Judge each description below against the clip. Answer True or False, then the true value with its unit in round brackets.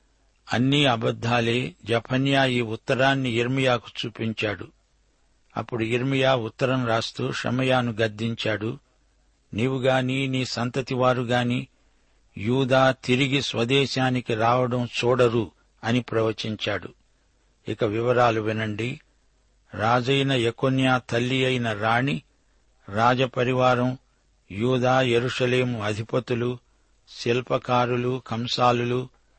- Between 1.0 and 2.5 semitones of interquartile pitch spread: True (2.1 semitones)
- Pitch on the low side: True (125 Hz)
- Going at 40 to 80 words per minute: True (75 wpm)